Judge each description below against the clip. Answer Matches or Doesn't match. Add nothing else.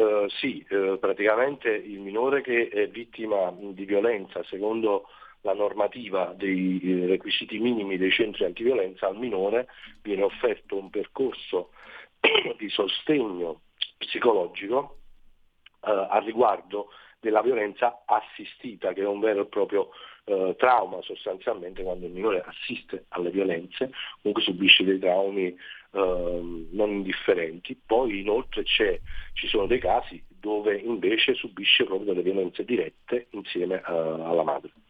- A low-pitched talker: Matches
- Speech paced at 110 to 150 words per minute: Matches